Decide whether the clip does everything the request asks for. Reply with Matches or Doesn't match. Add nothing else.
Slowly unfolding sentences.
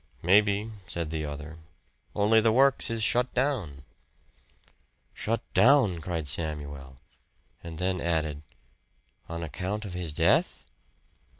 Matches